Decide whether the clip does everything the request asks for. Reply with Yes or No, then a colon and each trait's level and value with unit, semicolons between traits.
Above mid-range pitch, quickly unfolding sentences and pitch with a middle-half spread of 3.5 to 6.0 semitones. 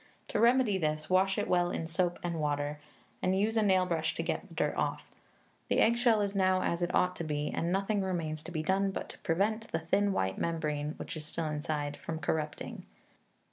No: medium, 175 Hz; fast, 215 wpm; average, 3.9 semitones